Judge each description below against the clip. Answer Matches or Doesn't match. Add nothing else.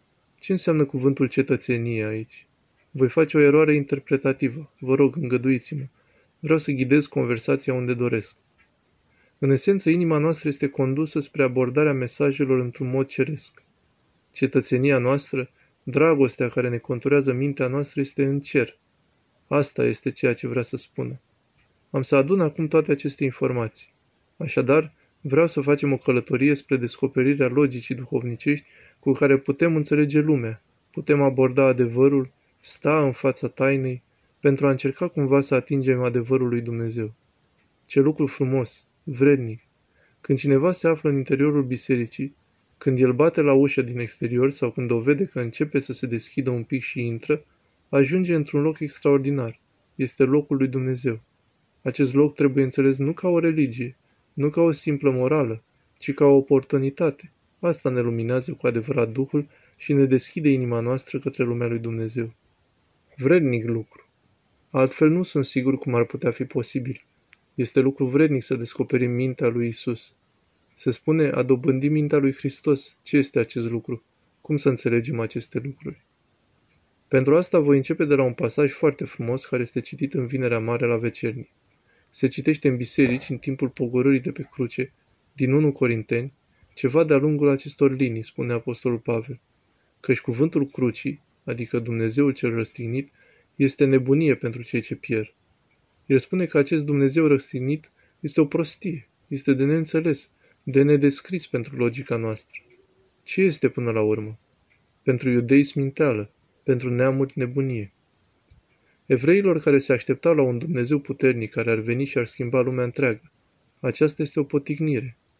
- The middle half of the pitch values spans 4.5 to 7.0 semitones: Doesn't match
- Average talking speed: Matches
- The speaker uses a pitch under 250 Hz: Matches